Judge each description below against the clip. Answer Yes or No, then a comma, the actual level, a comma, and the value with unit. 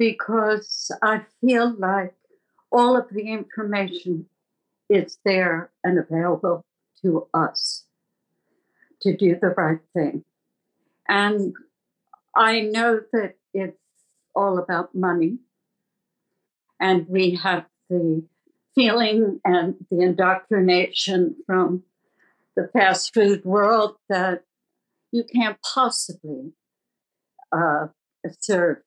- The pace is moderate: No, slow, 95 wpm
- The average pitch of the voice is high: Yes, high, 195 Hz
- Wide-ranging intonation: No, average, 3.6 semitones